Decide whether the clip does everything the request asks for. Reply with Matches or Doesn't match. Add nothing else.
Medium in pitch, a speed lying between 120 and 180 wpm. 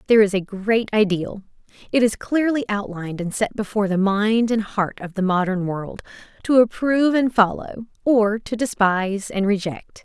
Doesn't match